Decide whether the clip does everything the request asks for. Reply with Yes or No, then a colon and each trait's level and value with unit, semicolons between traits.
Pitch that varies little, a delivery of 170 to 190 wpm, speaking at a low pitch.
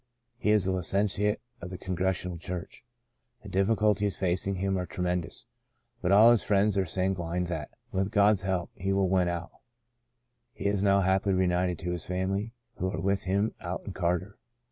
Yes: narrow, 1.8 semitones; average, 180 wpm; very low, 95 Hz